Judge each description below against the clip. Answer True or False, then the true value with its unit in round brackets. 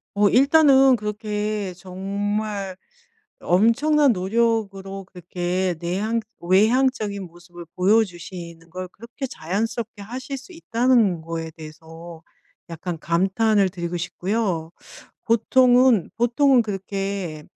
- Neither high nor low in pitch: False (200 Hz)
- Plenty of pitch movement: False (4.6 semitones)